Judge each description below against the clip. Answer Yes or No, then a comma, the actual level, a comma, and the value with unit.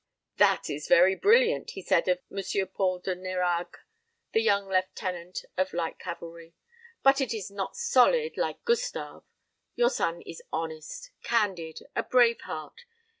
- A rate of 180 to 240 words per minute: No, average, 145 wpm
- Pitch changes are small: No, wide, 5.5 semitones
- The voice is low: No, medium, 185 Hz